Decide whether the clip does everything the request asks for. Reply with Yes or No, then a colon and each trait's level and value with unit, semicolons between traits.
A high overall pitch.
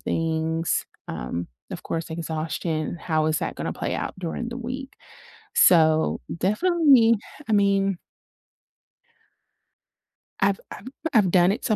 No: medium, 180 Hz